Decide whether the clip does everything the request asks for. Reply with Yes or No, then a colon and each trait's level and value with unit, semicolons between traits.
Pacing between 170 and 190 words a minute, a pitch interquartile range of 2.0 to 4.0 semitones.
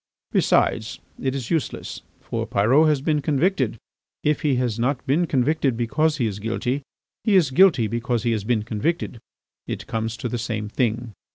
No: average, 175 wpm; average, 4.7 semitones